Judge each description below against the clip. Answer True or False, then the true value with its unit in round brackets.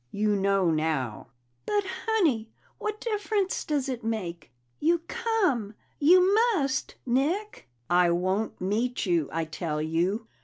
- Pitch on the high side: True (220 Hz)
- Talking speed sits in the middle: False (125 wpm)